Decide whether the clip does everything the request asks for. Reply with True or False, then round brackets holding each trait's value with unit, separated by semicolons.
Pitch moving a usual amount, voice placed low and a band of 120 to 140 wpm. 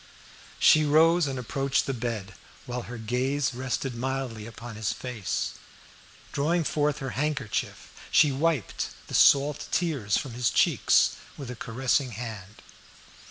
True (3.6 semitones; 130 Hz; 135 wpm)